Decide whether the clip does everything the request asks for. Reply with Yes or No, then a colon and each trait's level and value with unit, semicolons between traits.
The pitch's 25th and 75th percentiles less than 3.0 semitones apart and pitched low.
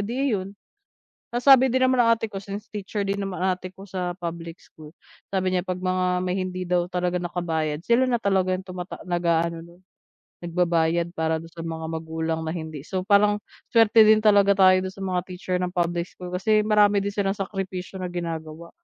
No: narrow, 2.6 semitones; medium, 185 Hz